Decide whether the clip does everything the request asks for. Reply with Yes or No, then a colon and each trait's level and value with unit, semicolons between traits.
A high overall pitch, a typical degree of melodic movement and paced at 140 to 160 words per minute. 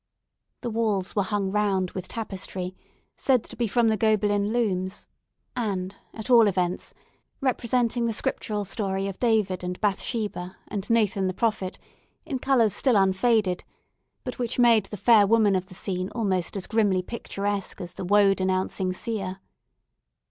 Yes: high, 205 Hz; average, 3.3 semitones; average, 155 wpm